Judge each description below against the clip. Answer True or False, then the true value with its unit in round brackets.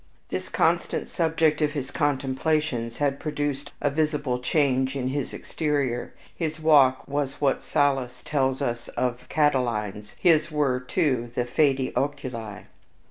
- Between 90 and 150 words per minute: True (135 wpm)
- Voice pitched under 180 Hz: True (140 Hz)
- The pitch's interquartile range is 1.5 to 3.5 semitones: True (2.9 semitones)